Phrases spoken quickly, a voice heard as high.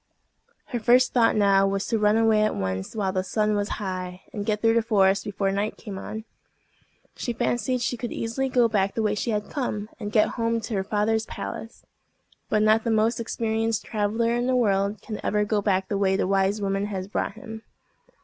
Yes: fast, 210 wpm; high, 215 Hz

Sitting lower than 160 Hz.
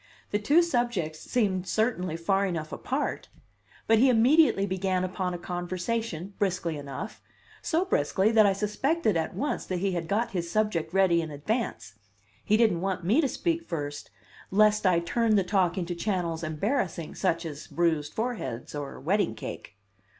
No: high, 190 Hz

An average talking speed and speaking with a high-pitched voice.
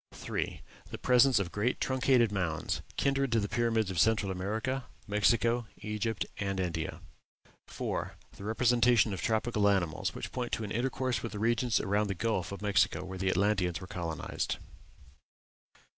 No: average, 160 wpm; low, 105 Hz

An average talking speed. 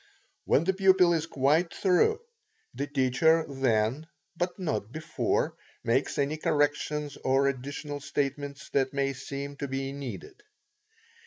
No: slow, 130 wpm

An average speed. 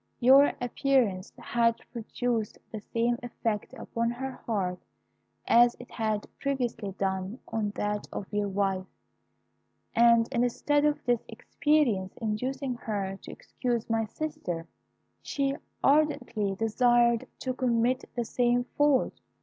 No: slow, 120 wpm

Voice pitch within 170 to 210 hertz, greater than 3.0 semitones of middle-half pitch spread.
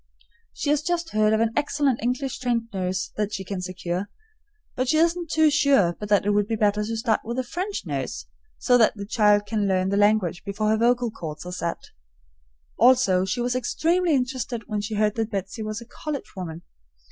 No: high, 220 Hz; average, 4.1 semitones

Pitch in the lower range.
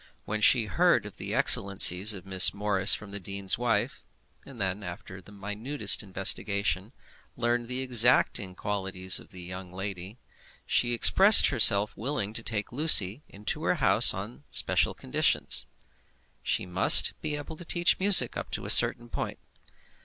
Yes: low, 105 Hz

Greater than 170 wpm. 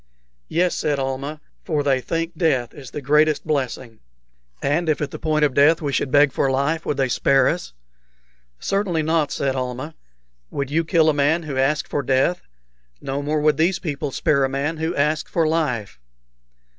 Yes: average, 180 wpm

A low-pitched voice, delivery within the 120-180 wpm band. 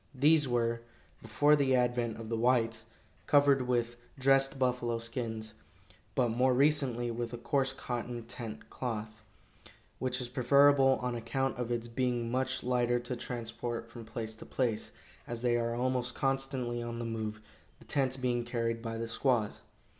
Yes: low, 120 Hz; average, 160 wpm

